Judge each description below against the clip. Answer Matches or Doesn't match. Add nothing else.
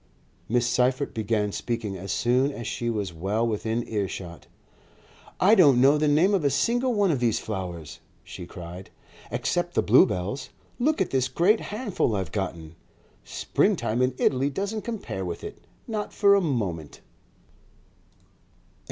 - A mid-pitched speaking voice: Doesn't match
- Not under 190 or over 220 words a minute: Doesn't match